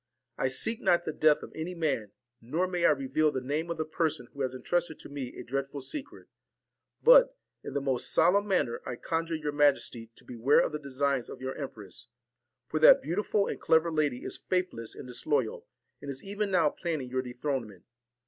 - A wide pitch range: No, average, 4.4 semitones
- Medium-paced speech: Yes, average, 195 wpm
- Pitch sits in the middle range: Yes, medium, 145 Hz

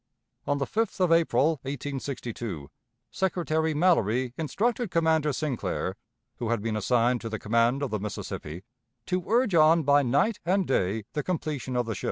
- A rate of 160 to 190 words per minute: Yes, average, 165 wpm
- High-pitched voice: No, medium, 140 Hz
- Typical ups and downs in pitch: No, wide, 6.0 semitones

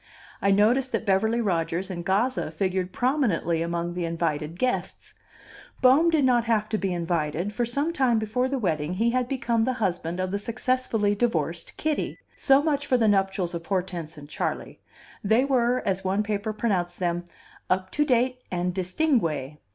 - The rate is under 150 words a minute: No, average, 175 wpm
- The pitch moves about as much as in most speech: No, wide, 6.1 semitones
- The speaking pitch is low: No, high, 205 Hz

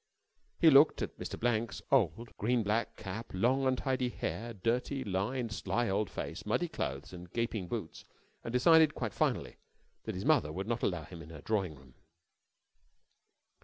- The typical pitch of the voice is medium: No, low, 115 Hz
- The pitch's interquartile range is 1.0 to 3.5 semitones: No, average, 5.0 semitones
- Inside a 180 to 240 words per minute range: No, average, 165 wpm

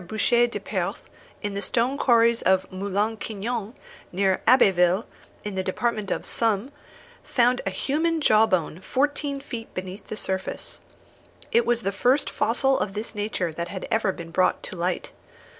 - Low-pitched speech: No, high, 215 Hz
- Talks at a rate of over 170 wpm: No, average, 160 wpm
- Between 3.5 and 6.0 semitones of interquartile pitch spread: Yes, average, 4.1 semitones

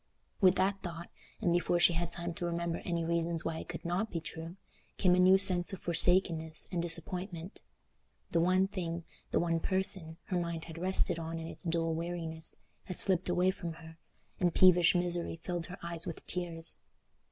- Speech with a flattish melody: Yes, narrow, 1.6 semitones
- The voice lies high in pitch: No, medium, 170 Hz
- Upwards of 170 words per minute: Yes, average, 180 wpm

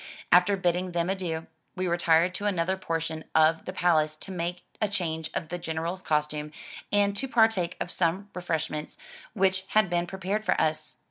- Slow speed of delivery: No, average, 175 wpm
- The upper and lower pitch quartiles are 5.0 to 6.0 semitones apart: No, average, 2.8 semitones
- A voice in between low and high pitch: Yes, medium, 175 Hz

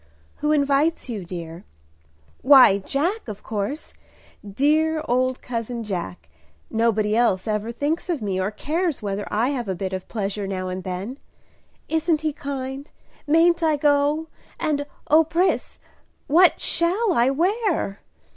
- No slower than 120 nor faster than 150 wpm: Yes, average, 140 wpm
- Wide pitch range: Yes, wide, 7.1 semitones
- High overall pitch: Yes, very high, 265 Hz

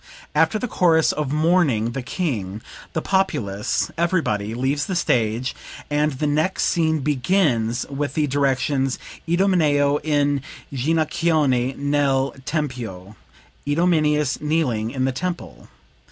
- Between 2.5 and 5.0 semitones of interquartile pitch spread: Yes, average, 4.0 semitones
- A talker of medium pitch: Yes, medium, 145 Hz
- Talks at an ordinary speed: No, slow, 115 wpm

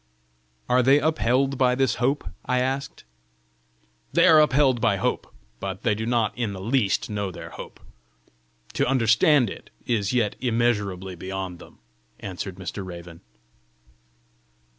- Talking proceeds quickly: No, average, 140 wpm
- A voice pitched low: Yes, low, 115 Hz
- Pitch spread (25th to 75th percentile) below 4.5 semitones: No, average, 4.9 semitones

